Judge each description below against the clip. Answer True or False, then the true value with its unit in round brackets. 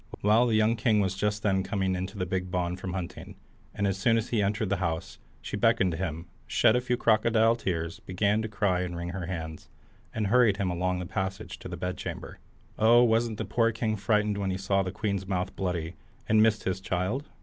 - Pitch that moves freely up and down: False (3.0 semitones)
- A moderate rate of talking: False (220 wpm)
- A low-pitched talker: True (100 Hz)